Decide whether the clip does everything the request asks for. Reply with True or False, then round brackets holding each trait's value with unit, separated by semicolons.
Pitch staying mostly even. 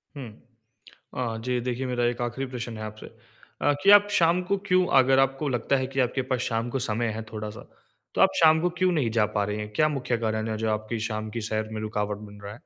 False (3.8 semitones)